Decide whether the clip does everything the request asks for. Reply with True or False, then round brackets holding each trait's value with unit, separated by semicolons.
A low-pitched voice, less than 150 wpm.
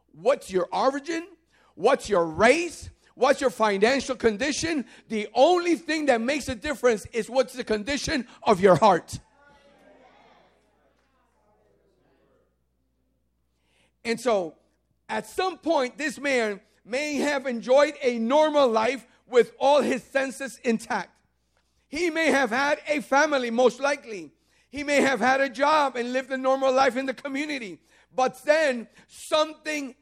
False (265 Hz; 135 wpm)